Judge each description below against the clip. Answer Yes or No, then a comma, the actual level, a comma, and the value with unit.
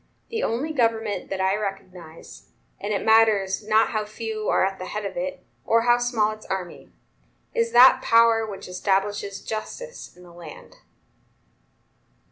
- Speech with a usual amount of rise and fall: Yes, average, 3.0 semitones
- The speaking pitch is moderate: No, high, 215 Hz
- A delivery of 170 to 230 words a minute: No, average, 155 wpm